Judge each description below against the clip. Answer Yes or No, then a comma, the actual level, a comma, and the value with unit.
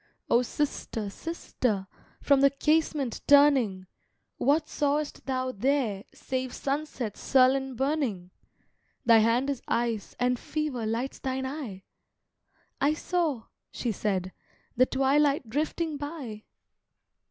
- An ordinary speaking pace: No, slow, 110 wpm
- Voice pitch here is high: Yes, very high, 265 Hz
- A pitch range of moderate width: Yes, average, 4.0 semitones